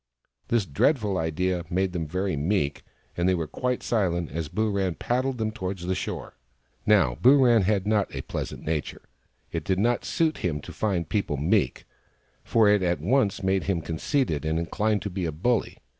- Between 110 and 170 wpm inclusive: No, average, 180 wpm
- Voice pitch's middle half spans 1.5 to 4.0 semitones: No, average, 4.5 semitones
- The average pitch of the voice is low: Yes, very low, 95 Hz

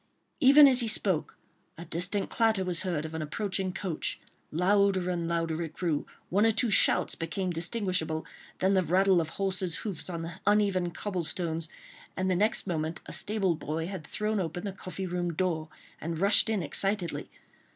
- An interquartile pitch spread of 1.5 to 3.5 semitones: Yes, average, 3.1 semitones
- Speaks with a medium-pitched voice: Yes, medium, 180 Hz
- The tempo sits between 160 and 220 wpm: Yes, average, 180 wpm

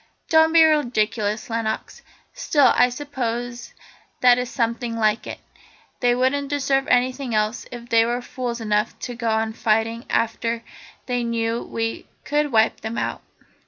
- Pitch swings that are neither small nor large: No, narrow, 2.0 semitones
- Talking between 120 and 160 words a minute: Yes, average, 150 wpm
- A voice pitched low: No, high, 240 Hz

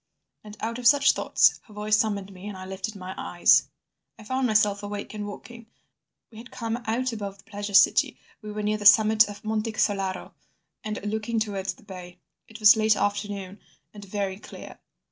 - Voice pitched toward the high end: Yes, high, 210 Hz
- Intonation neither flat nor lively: No, narrow, 1.5 semitones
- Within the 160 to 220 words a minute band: Yes, average, 195 wpm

